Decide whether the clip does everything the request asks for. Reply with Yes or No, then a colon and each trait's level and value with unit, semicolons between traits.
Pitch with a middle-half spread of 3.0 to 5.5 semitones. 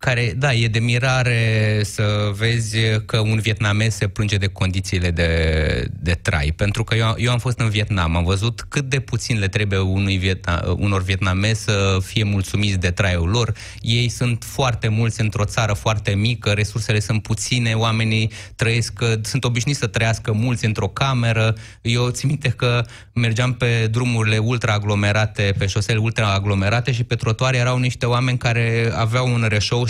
No: narrow, 2.6 semitones